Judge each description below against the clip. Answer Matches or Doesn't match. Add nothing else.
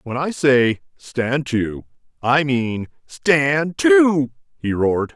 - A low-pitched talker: Matches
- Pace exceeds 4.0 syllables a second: Doesn't match